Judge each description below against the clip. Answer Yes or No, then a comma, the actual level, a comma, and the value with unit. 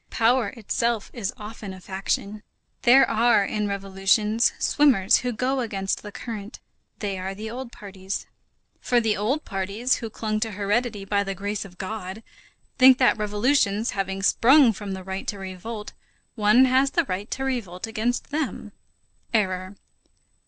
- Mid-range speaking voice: No, high, 210 Hz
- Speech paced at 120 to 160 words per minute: Yes, average, 155 wpm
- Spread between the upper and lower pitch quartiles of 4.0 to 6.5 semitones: No, average, 3.5 semitones